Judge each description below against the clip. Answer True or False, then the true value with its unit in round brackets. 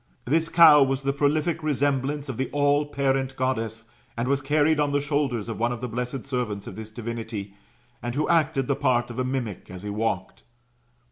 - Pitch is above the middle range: False (135 Hz)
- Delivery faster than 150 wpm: True (195 wpm)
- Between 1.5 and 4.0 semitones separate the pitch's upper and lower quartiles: True (3.6 semitones)